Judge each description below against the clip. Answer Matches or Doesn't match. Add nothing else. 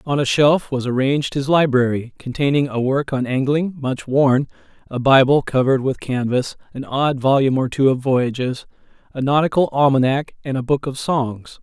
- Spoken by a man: Matches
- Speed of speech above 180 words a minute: Doesn't match